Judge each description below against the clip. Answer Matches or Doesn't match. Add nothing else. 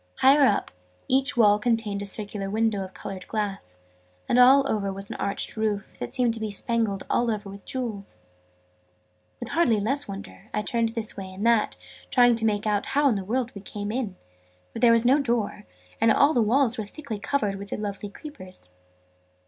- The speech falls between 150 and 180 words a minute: Doesn't match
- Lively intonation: Doesn't match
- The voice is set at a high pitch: Matches